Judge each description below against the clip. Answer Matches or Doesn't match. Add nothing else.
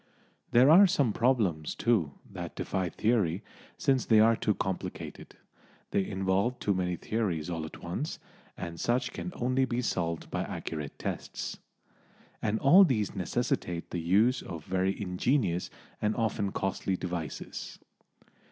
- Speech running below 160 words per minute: Matches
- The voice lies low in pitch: Matches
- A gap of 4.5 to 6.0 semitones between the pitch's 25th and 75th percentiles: Matches